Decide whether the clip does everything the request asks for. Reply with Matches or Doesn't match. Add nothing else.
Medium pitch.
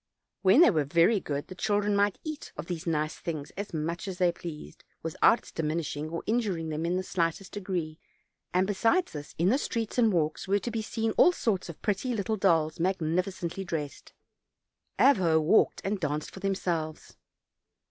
Matches